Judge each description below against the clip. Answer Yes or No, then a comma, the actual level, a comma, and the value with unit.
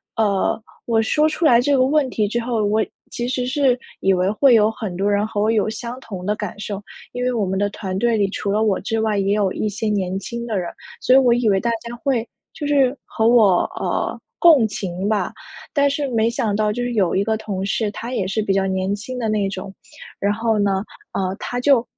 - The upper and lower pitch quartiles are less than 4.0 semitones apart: Yes, average, 3.4 semitones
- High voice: Yes, high, 220 Hz